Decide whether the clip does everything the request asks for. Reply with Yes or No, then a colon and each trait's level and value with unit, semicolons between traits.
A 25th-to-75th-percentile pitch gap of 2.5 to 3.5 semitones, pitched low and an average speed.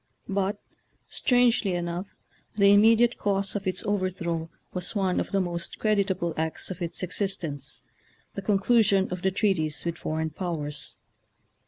No: average, 2.9 semitones; high, 190 Hz; average, 155 wpm